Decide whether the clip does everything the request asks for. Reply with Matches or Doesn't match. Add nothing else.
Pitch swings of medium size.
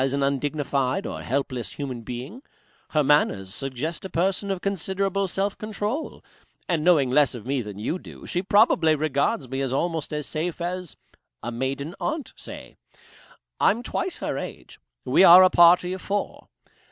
Doesn't match